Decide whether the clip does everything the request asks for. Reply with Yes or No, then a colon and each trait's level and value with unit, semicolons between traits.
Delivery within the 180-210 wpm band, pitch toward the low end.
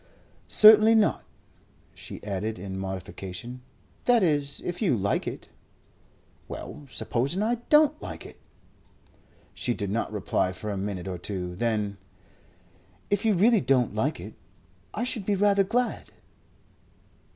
No: slow, 135 wpm; low, 125 Hz